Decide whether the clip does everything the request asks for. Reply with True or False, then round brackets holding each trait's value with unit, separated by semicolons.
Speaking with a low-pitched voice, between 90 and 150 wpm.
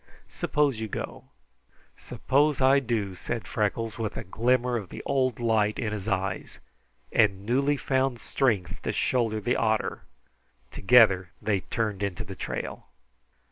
True (115 Hz; 140 wpm)